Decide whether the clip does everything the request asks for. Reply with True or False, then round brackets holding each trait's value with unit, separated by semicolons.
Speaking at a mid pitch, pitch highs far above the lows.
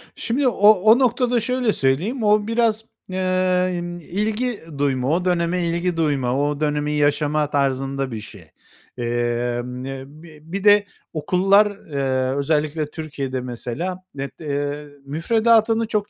True (160 Hz; 6.9 semitones)